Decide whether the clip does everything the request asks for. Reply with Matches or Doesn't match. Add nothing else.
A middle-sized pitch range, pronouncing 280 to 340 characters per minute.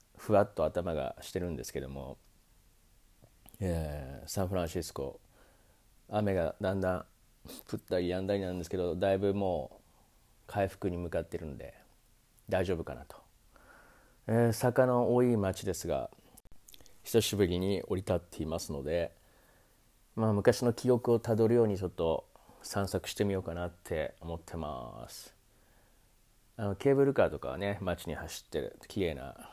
Matches